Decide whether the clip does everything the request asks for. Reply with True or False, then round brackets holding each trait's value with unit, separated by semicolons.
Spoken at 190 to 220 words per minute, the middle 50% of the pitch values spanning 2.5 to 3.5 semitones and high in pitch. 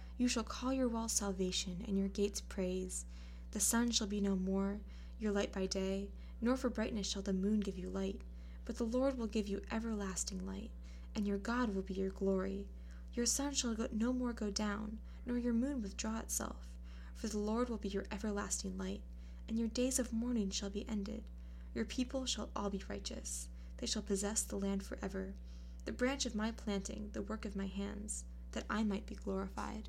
True (200 wpm; 3.0 semitones; 200 Hz)